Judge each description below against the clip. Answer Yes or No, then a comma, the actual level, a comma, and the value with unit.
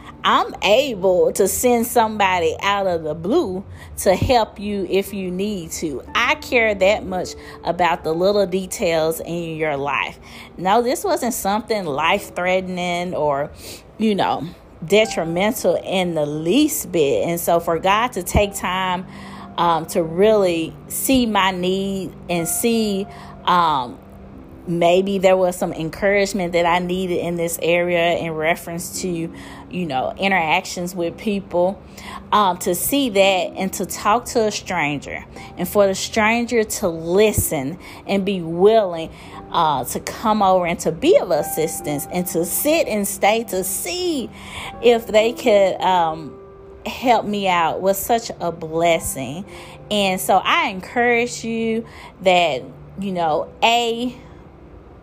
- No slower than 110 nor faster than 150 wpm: Yes, average, 145 wpm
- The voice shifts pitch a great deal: No, average, 4.0 semitones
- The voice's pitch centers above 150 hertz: Yes, high, 190 Hz